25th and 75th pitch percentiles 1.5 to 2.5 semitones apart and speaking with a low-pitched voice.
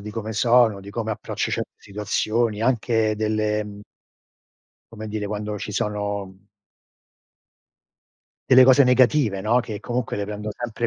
Yes: narrow, 2.2 semitones; low, 110 Hz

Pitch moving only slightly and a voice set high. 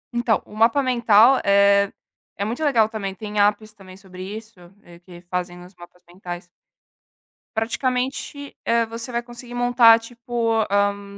No: average, 3.5 semitones; high, 220 Hz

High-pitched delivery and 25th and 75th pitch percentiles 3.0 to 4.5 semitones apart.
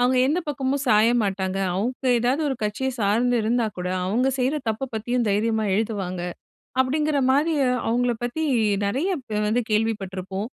Yes: high, 235 Hz; average, 3.8 semitones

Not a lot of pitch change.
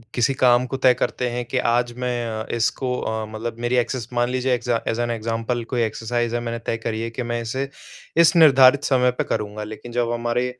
Yes: narrow, 1.5 semitones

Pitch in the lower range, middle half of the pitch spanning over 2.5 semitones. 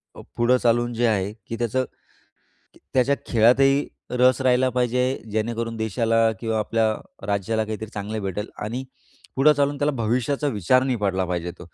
Yes: low, 115 Hz; average, 2.9 semitones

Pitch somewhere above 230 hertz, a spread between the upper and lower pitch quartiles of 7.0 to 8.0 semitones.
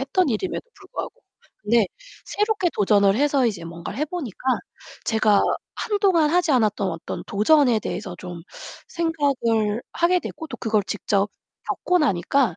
Yes: high, 240 Hz; wide, 7.7 semitones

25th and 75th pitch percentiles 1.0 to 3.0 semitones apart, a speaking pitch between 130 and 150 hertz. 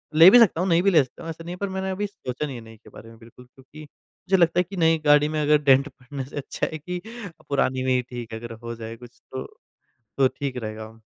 No: average, 5.2 semitones; medium, 140 Hz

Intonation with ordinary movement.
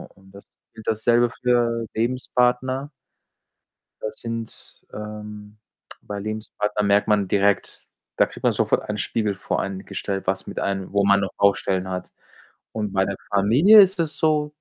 Yes: average, 3.2 semitones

